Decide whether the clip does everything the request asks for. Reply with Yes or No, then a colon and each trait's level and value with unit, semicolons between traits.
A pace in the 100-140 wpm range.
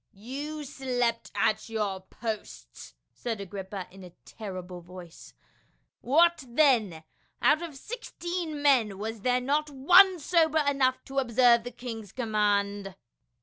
Yes: slow, 135 wpm